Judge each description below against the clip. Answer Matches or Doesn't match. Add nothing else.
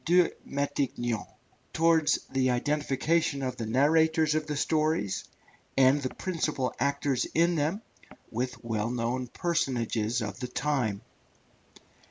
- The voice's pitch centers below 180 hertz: Matches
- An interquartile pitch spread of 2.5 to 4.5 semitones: Matches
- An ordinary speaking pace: Doesn't match